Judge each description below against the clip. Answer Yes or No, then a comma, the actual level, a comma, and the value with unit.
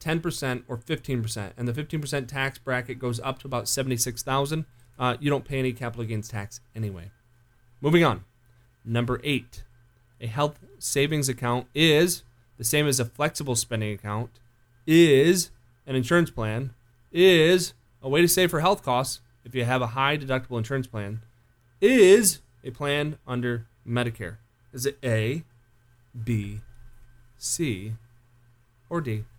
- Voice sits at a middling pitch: No, low, 120 Hz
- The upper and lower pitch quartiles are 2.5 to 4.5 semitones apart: Yes, average, 3.0 semitones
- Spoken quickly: No, average, 145 wpm